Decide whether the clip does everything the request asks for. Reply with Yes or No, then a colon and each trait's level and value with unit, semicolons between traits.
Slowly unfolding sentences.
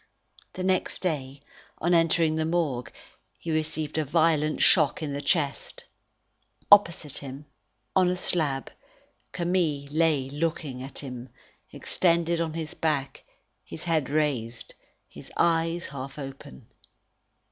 Yes: slow, 125 wpm